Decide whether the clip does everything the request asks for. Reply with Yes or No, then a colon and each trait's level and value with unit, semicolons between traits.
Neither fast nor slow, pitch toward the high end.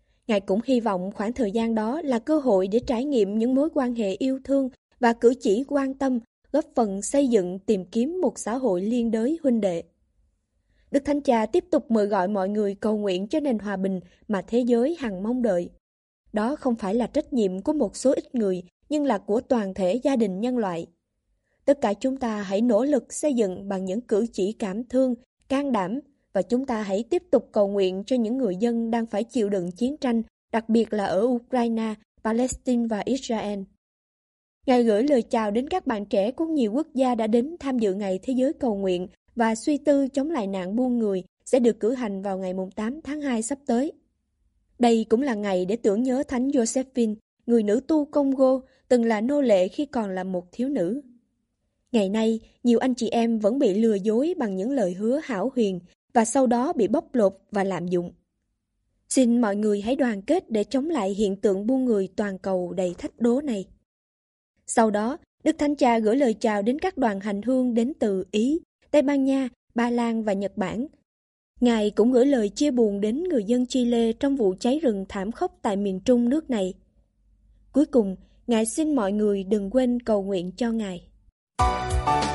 Yes: average, 210 wpm; high, 230 Hz